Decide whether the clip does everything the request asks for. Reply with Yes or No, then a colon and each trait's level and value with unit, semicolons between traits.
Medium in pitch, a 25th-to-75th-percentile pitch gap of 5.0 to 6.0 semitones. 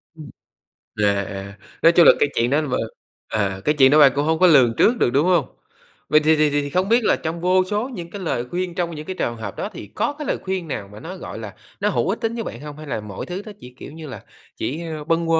Yes: medium, 155 Hz; wide, 5.5 semitones